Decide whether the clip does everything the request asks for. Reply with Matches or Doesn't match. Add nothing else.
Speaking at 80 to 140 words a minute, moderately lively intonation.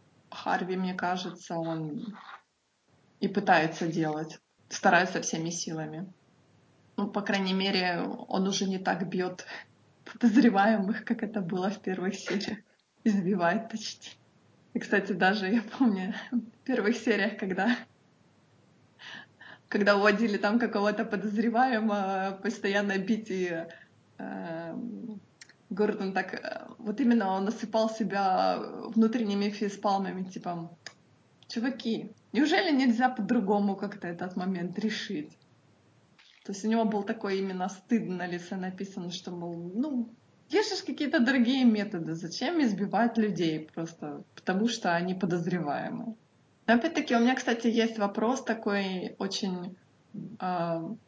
Matches